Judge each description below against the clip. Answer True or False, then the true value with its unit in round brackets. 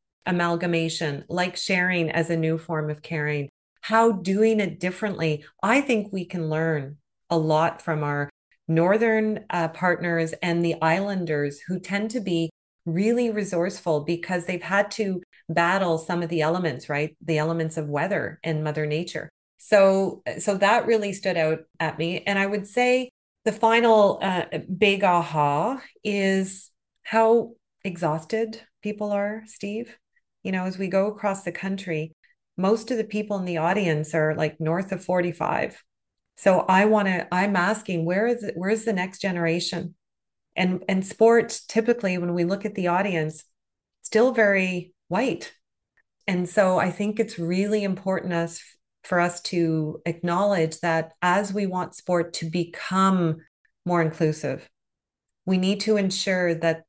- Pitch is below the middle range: False (180 Hz)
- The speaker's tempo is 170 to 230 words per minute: False (155 wpm)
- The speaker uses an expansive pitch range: False (3.7 semitones)